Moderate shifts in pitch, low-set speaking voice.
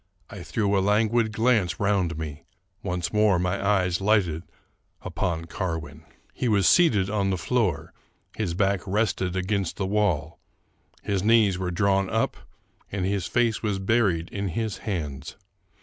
Yes: average, 3.0 semitones; very low, 95 Hz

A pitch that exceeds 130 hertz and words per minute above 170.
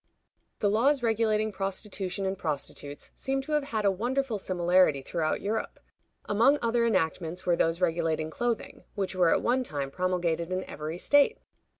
No: high, 190 Hz; average, 160 wpm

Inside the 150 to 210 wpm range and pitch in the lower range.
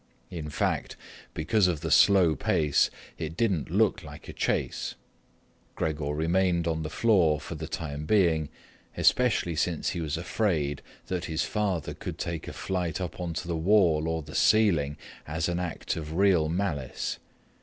Yes: average, 160 wpm; very low, 80 Hz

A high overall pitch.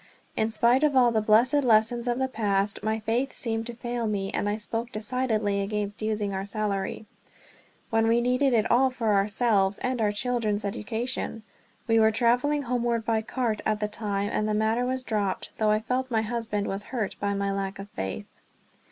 Yes: high, 220 Hz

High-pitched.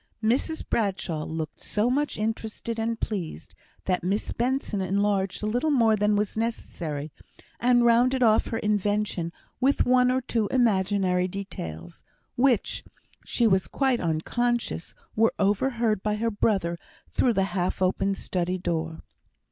Yes: high, 210 Hz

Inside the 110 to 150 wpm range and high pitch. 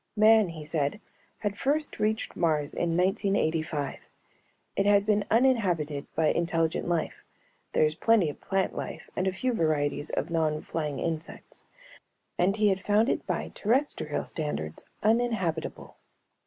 No: average, 140 wpm; medium, 175 Hz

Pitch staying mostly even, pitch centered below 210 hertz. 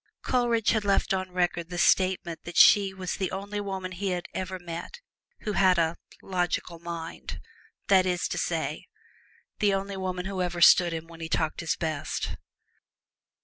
Yes: narrow, 2.1 semitones; medium, 185 Hz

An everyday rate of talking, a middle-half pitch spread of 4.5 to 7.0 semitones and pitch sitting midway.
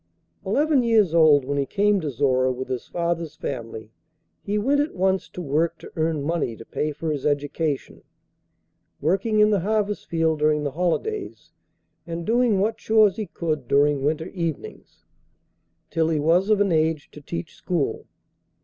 Yes: average, 165 wpm; wide, 5.4 semitones; medium, 165 Hz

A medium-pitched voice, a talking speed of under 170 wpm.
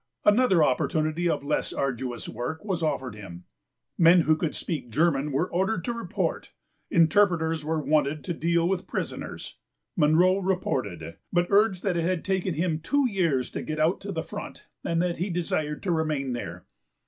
No: medium, 165 Hz; average, 175 wpm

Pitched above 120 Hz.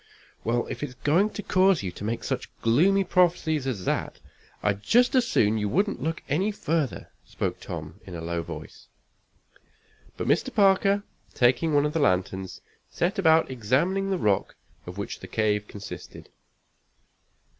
Yes: medium, 140 Hz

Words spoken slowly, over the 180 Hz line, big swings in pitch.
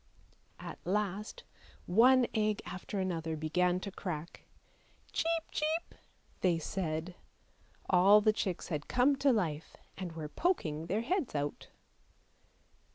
Yes: slow, 130 wpm; high, 190 Hz; wide, 5.8 semitones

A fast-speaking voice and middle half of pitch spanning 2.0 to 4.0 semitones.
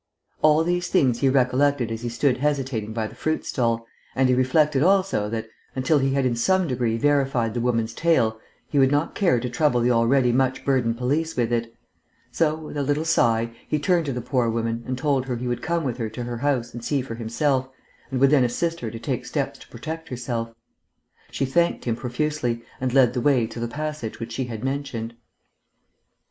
Yes: fast, 210 wpm; average, 3.7 semitones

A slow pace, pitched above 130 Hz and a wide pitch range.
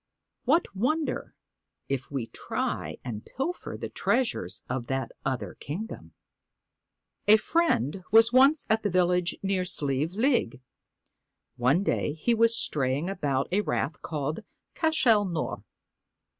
Yes: slow, 130 wpm; medium, 185 Hz; wide, 8.8 semitones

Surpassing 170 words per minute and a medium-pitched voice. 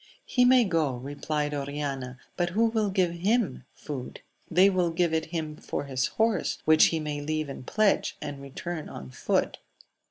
Yes: average, 180 wpm; medium, 155 Hz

